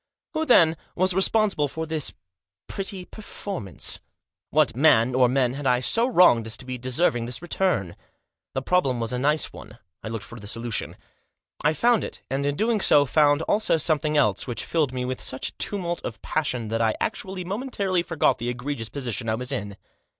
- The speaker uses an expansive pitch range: Yes, wide, 6.7 semitones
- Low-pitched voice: No, medium, 145 Hz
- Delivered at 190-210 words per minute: Yes, average, 195 wpm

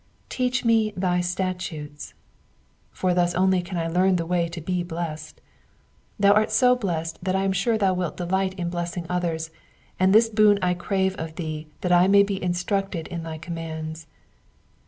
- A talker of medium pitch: Yes, medium, 180 Hz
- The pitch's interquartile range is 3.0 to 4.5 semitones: No, narrow, 2.5 semitones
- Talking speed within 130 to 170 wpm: No, average, 180 wpm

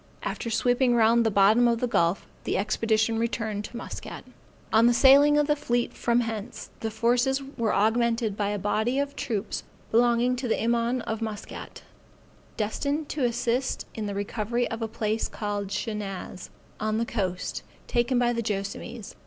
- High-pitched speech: Yes, high, 230 Hz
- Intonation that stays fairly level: Yes, narrow, 2.3 semitones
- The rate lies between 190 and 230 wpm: No, average, 170 wpm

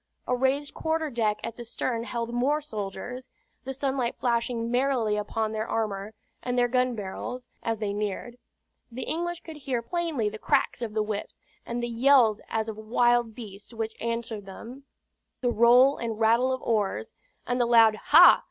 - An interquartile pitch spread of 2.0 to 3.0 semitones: Yes, narrow, 2.6 semitones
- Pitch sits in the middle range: No, high, 235 Hz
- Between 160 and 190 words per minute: Yes, average, 175 wpm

